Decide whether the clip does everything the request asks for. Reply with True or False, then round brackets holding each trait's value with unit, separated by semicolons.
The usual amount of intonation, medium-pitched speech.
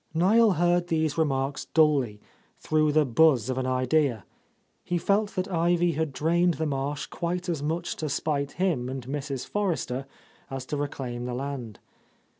True (4.4 semitones; 150 Hz)